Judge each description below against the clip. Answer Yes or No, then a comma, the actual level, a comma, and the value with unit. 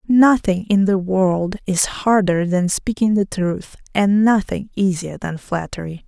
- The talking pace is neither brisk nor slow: Yes, average, 150 wpm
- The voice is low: No, high, 195 Hz